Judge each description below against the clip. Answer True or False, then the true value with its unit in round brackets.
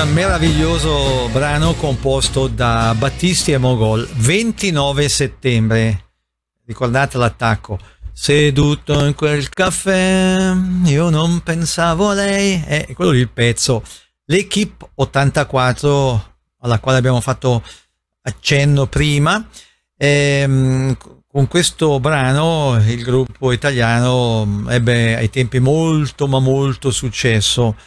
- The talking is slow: True (105 wpm)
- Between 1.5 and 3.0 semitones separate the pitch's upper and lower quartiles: False (4.2 semitones)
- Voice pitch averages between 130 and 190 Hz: True (135 Hz)